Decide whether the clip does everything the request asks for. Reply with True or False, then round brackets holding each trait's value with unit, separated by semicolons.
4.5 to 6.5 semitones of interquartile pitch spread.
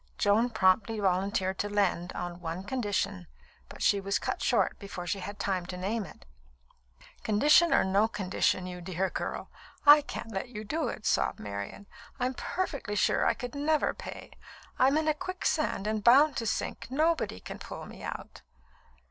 True (5.4 semitones)